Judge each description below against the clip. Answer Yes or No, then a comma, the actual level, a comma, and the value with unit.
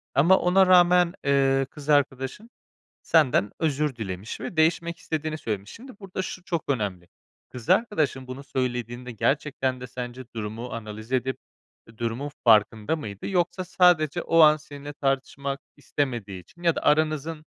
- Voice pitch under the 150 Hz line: Yes, medium, 140 Hz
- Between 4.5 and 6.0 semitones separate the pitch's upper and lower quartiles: Yes, average, 4.9 semitones